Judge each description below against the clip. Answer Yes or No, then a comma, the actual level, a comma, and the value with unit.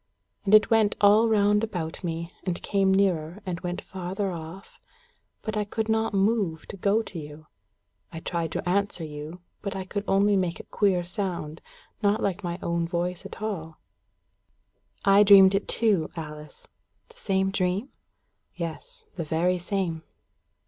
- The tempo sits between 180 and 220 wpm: No, average, 160 wpm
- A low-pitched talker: No, high, 190 Hz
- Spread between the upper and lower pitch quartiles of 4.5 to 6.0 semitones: No, average, 3.2 semitones